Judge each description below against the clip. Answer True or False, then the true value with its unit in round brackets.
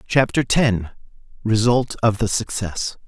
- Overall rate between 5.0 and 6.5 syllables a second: False (3.9 syllables/s)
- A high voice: False (115 Hz)